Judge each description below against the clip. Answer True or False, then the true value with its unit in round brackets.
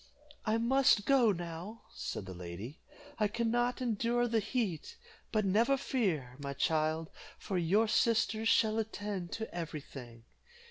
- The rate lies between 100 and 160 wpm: True (145 wpm)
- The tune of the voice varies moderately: False (6.2 semitones)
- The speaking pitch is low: False (210 Hz)